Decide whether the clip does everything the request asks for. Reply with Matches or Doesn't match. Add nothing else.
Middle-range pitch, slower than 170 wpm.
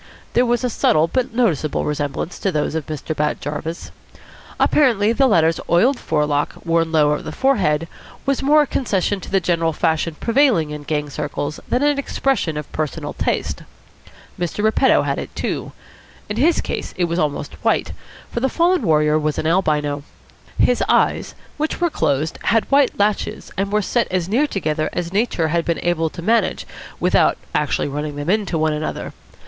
Doesn't match